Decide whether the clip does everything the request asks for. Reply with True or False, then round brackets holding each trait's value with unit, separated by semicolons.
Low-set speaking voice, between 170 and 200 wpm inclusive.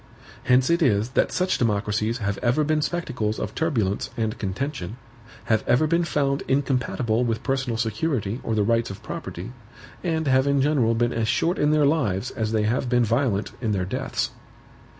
True (120 Hz; 180 wpm)